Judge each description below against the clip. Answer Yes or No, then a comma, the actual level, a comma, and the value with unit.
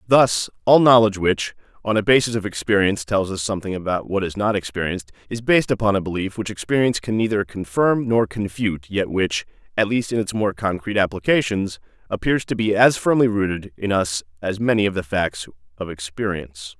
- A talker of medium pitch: No, low, 100 Hz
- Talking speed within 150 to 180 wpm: No, average, 190 wpm